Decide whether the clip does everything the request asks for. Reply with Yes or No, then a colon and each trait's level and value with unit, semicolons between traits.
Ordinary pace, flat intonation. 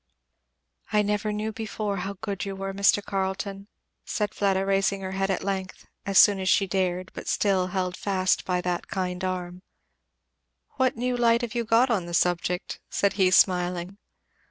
Yes: average, 175 wpm; narrow, 2.0 semitones